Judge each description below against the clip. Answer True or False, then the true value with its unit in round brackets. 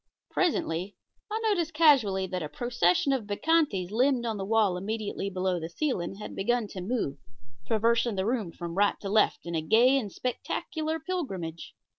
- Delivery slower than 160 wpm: False (170 wpm)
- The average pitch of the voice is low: False (215 Hz)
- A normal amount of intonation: False (5.7 semitones)